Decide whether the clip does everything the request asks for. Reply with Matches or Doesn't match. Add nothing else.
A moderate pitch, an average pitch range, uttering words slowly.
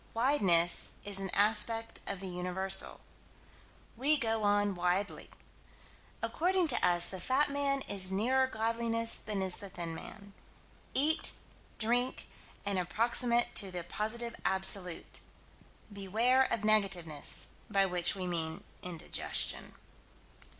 Doesn't match